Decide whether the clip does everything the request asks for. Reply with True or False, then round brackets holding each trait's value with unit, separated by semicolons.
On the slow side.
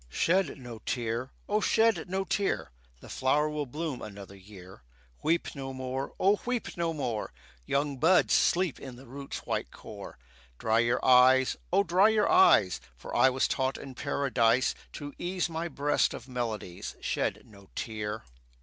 False (160 wpm)